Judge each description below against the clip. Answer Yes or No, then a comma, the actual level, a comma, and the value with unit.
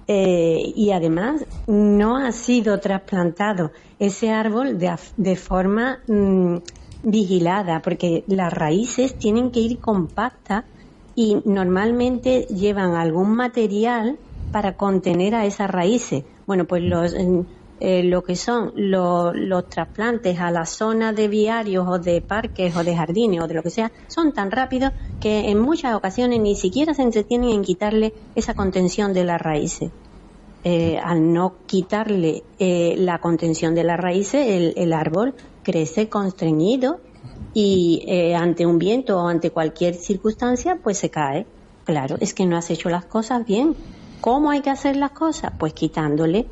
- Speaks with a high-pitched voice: Yes, high, 195 Hz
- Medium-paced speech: Yes, average, 155 wpm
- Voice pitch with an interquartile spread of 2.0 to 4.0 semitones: No, average, 4.6 semitones